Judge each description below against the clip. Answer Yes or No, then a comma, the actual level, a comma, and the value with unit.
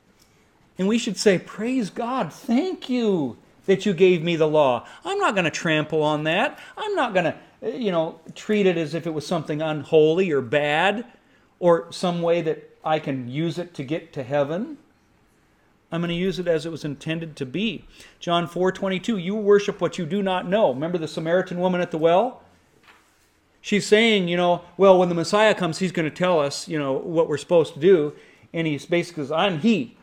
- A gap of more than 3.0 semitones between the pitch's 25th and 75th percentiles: Yes, average, 4.0 semitones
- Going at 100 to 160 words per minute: No, fast, 205 wpm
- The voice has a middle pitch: Yes, medium, 175 Hz